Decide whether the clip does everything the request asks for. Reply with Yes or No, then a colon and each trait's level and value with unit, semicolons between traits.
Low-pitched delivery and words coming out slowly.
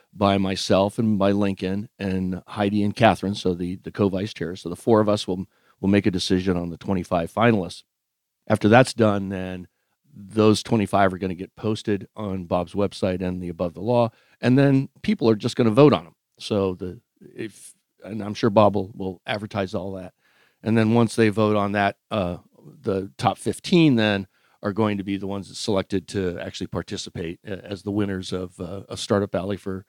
No: low, 100 Hz; fast, 205 wpm